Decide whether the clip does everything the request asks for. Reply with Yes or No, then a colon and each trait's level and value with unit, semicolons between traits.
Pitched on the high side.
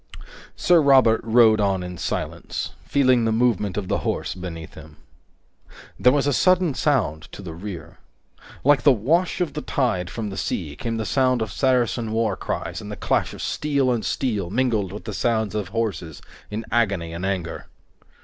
No: low, 110 Hz